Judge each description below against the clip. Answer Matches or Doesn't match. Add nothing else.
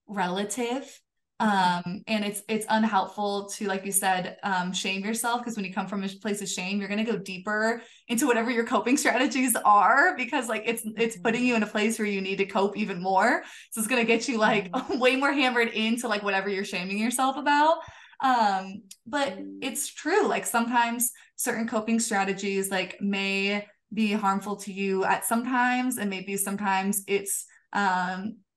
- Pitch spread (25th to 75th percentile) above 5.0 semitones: Doesn't match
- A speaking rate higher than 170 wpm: Matches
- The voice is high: Matches